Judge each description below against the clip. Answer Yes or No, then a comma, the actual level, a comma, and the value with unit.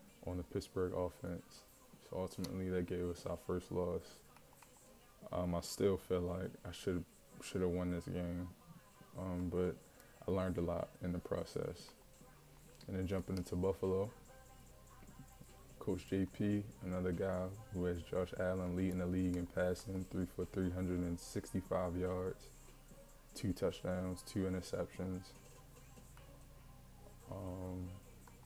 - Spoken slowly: Yes, slow, 125 wpm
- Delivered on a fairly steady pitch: Yes, narrow, 0.9 semitones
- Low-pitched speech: Yes, very low, 90 Hz